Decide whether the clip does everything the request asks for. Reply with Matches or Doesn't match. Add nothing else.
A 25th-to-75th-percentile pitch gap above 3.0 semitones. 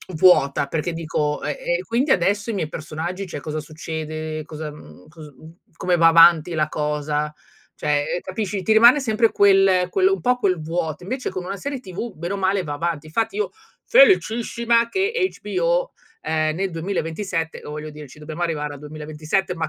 Matches